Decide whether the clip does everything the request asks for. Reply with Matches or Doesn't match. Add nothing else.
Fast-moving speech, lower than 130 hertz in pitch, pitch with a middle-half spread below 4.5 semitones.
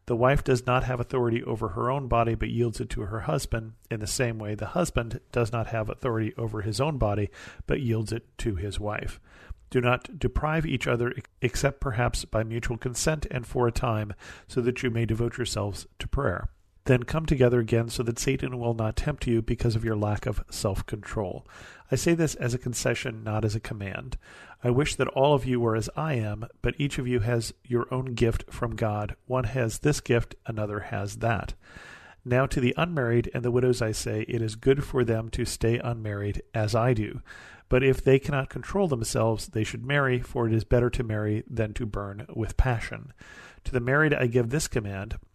Matches